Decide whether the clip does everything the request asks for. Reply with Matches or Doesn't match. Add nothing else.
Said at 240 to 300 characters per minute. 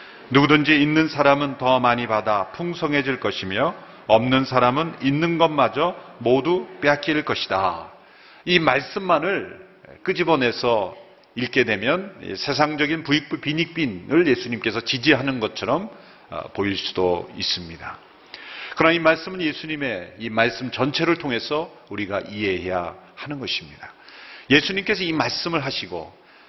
Matches